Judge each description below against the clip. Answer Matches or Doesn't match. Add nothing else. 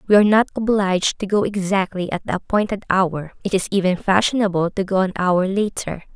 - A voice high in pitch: Matches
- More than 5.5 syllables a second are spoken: Matches